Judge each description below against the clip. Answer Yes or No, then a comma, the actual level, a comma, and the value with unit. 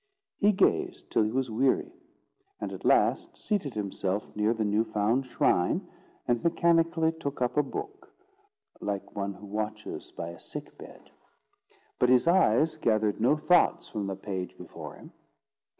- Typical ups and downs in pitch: No, wide, 7.5 semitones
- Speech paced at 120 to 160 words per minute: Yes, average, 155 wpm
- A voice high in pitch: No, low, 115 Hz